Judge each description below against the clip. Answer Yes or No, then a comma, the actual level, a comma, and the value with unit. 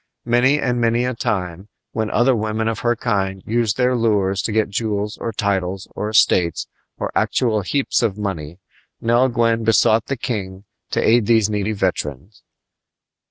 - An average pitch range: Yes, average, 3.2 semitones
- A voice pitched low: Yes, low, 110 Hz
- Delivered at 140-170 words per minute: Yes, average, 160 wpm